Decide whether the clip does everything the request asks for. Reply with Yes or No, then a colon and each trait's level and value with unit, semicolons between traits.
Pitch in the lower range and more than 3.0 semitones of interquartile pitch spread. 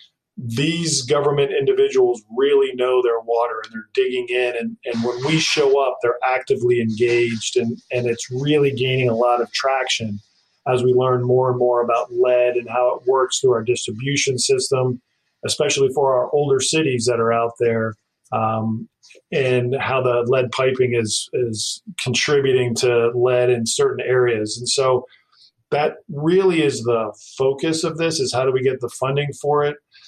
Yes: low, 125 Hz; average, 3.5 semitones